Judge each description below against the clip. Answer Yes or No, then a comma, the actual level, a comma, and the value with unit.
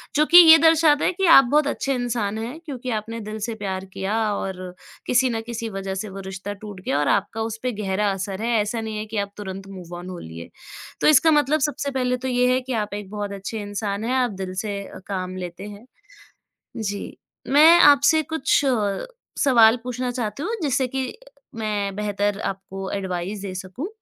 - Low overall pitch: No, high, 215 Hz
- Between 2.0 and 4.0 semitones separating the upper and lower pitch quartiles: No, average, 4.6 semitones